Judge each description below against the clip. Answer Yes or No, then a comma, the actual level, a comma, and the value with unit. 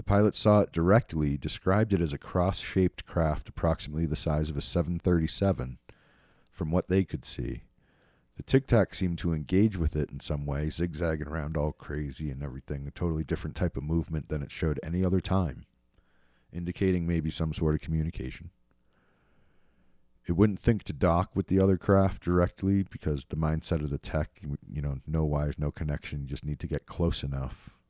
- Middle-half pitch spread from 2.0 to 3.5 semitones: No, average, 3.9 semitones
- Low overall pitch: Yes, very low, 80 Hz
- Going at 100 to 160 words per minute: No, average, 185 wpm